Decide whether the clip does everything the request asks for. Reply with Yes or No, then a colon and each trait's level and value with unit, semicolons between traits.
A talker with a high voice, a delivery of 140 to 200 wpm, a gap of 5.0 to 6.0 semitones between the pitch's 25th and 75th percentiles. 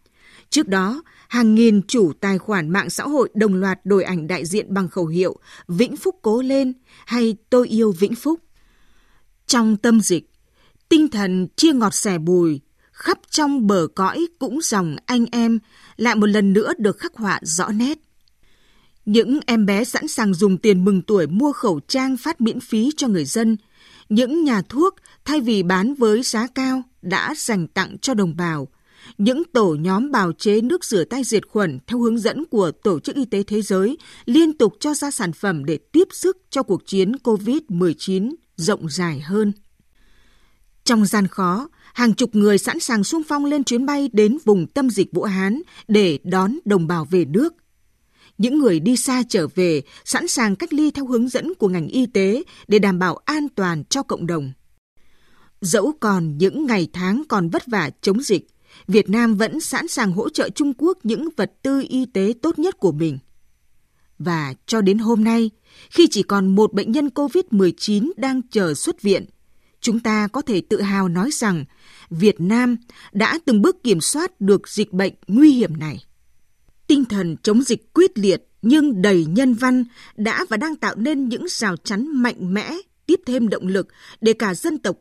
Yes: high, 220 Hz; average, 190 wpm; wide, 5.5 semitones